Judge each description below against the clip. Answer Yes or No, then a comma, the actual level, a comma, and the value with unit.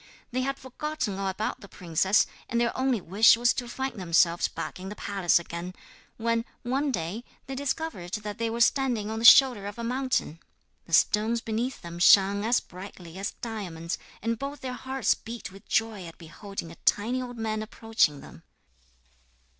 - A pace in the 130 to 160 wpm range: No, average, 180 wpm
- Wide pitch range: No, average, 4.4 semitones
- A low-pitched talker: No, high, 220 Hz